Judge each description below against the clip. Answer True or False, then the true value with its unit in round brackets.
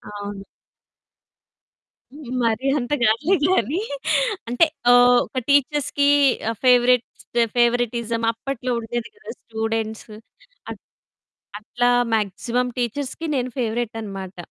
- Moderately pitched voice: False (240 Hz)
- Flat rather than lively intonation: True (2.3 semitones)